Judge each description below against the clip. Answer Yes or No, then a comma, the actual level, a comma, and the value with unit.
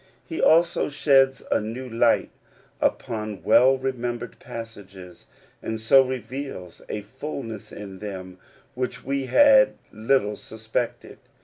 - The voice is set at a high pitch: No, low, 120 Hz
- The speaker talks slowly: Yes, slow, 110 wpm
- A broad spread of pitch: No, average, 4.1 semitones